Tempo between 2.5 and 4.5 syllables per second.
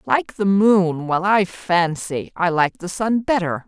Yes: 3.7 syllables/s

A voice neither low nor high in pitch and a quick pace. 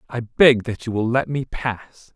No: low, 120 Hz; fast, 220 wpm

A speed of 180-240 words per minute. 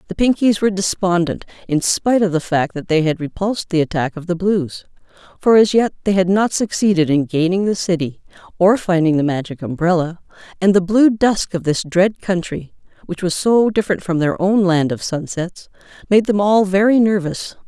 Yes: average, 185 wpm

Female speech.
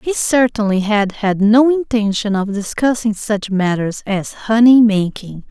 Yes: female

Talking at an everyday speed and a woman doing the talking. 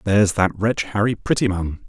No: average, 160 wpm; male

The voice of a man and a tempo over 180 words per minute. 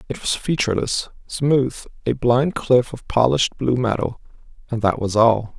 No: male; average, 150 wpm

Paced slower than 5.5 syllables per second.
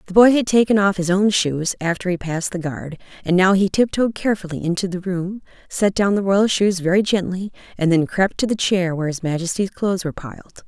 No: 5.9 syllables/s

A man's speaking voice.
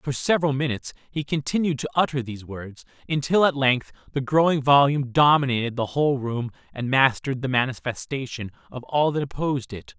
Yes: male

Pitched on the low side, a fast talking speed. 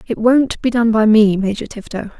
No: high, 220 Hz; fast, 220 wpm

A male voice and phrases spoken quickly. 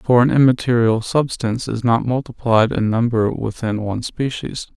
No: male; average, 150 wpm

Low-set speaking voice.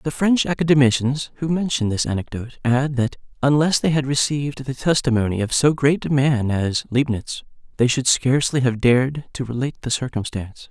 Yes: low, 130 Hz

